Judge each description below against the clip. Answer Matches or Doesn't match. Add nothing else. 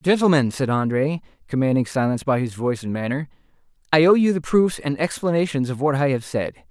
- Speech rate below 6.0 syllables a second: Doesn't match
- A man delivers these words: Matches